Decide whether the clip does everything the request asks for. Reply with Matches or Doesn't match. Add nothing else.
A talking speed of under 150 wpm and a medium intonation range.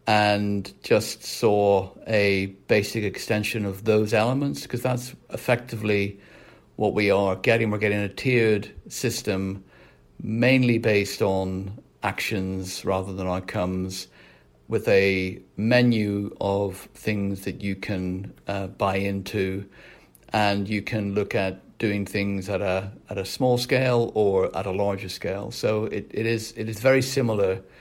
Doesn't match